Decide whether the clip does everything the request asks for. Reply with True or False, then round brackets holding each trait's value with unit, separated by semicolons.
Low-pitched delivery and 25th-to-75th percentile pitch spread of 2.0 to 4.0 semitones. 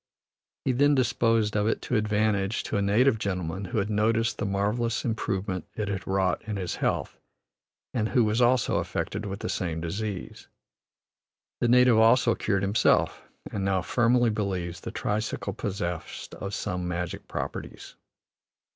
True (105 Hz; 2.8 semitones)